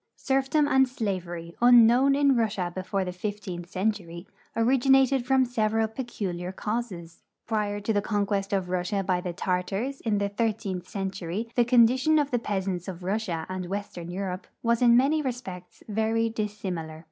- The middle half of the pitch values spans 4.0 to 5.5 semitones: Yes, average, 4.5 semitones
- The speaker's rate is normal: Yes, average, 155 wpm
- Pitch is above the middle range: Yes, high, 205 Hz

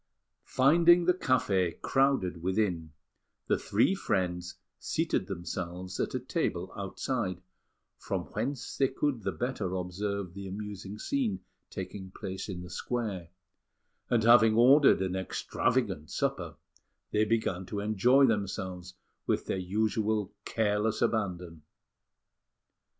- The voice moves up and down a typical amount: Yes, average, 4.4 semitones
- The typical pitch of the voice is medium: No, low, 105 Hz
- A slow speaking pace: Yes, slow, 115 wpm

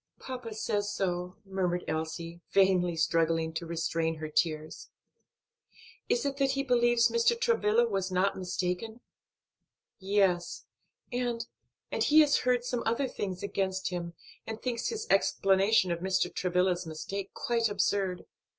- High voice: Yes, high, 195 Hz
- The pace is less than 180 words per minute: Yes, slow, 135 wpm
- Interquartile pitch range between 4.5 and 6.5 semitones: Yes, average, 5.0 semitones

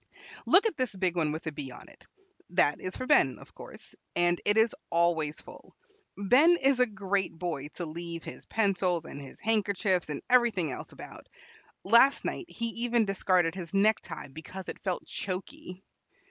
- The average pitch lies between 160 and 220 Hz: Yes, high, 190 Hz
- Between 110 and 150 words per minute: No, average, 175 wpm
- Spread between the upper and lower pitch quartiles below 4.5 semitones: No, average, 4.9 semitones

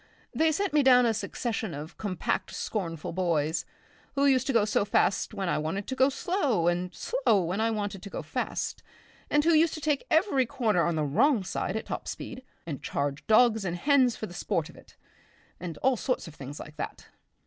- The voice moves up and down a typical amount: No, wide, 7.4 semitones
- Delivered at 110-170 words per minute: No, fast, 205 wpm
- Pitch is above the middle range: Yes, high, 215 Hz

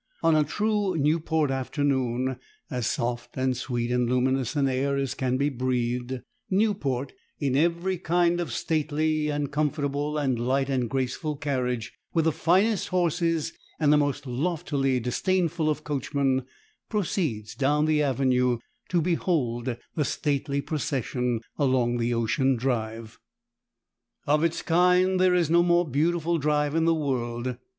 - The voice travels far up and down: No, average, 4.2 semitones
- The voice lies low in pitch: No, medium, 145 Hz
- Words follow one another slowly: No, average, 145 wpm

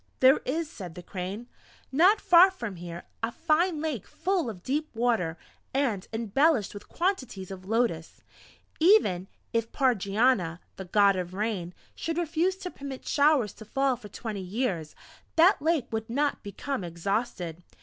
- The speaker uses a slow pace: No, average, 150 wpm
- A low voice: No, high, 230 Hz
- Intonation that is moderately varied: No, wide, 7.9 semitones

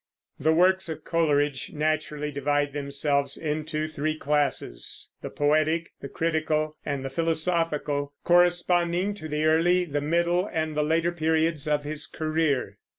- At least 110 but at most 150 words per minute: Yes, average, 140 wpm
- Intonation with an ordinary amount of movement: No, narrow, 2.1 semitones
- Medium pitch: Yes, medium, 155 Hz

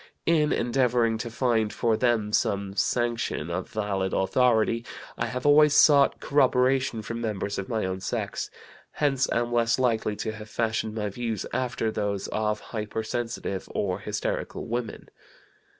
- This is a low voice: Yes, low, 115 Hz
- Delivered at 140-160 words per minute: Yes, average, 145 wpm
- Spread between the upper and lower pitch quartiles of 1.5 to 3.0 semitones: Yes, average, 2.7 semitones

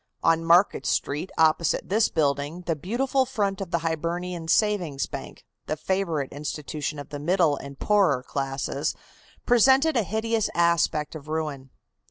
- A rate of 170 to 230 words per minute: No, average, 145 wpm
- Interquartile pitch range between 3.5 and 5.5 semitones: Yes, average, 4.9 semitones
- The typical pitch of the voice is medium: Yes, medium, 165 Hz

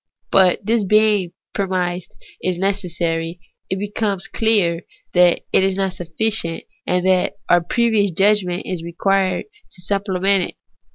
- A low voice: No, high, 190 Hz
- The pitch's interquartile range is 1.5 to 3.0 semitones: Yes, narrow, 2.4 semitones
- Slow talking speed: Yes, slow, 130 wpm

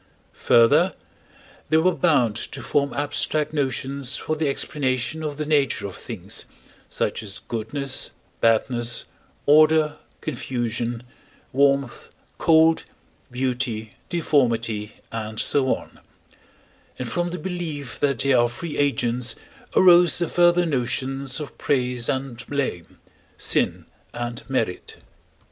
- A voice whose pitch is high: No, low, 135 Hz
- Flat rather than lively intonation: No, average, 4.1 semitones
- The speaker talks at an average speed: No, slow, 115 wpm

